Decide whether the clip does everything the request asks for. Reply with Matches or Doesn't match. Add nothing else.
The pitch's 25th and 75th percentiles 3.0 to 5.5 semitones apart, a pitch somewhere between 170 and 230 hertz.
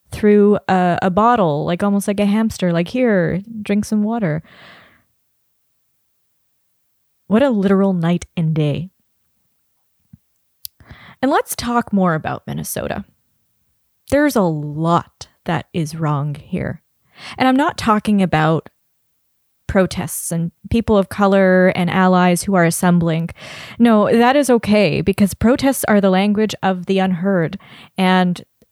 Matches